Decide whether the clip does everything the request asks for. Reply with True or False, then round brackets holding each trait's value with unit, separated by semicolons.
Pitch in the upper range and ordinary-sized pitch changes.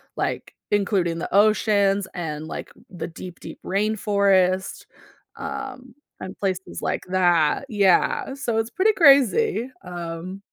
True (200 Hz; 4.4 semitones)